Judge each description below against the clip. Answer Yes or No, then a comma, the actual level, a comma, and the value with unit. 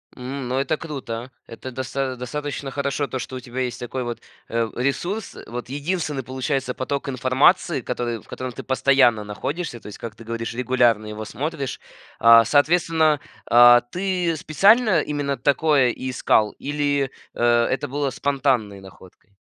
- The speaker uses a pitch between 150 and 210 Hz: No, low, 130 Hz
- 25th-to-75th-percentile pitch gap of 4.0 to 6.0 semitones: No, average, 3.3 semitones